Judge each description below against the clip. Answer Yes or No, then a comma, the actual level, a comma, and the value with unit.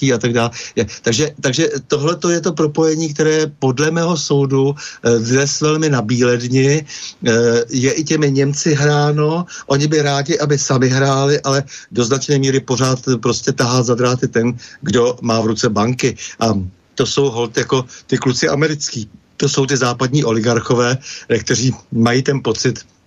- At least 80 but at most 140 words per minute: No, average, 160 wpm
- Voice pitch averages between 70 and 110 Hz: No, low, 135 Hz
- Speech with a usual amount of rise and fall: Yes, average, 3.3 semitones